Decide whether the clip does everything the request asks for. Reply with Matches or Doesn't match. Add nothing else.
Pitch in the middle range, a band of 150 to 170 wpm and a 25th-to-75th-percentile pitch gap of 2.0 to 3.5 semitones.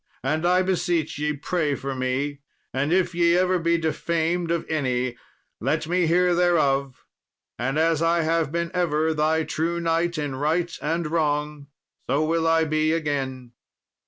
Matches